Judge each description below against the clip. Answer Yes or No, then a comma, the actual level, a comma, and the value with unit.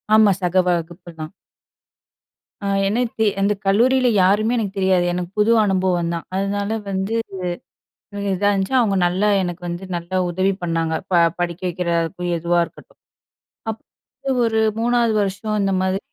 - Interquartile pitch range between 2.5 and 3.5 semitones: Yes, average, 3.1 semitones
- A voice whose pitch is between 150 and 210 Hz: Yes, high, 190 Hz